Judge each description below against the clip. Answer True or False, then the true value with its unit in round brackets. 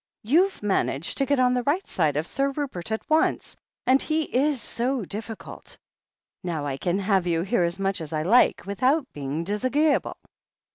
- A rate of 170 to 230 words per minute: True (190 wpm)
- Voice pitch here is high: True (220 Hz)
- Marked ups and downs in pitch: True (7.9 semitones)